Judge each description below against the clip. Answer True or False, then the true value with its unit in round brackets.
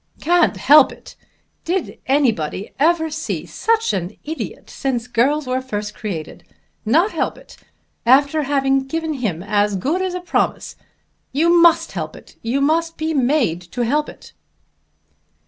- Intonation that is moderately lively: False (5.8 semitones)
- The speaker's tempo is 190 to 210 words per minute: False (145 wpm)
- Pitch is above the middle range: True (275 Hz)